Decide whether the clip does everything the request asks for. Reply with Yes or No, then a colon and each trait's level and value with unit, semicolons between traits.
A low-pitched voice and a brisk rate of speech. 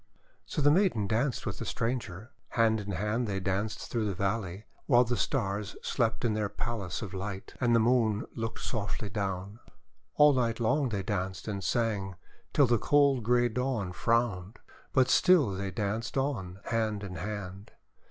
No: low, 110 Hz; average, 170 wpm